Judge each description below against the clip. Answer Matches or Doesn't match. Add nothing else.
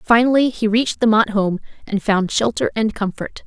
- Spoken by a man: Doesn't match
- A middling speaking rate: Matches